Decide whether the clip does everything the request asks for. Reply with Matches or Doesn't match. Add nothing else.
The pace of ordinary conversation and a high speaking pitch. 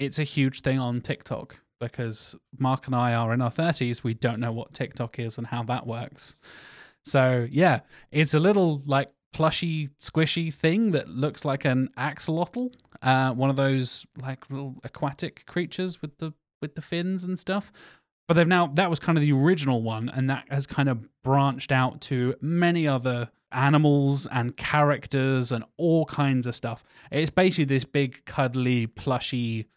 Doesn't match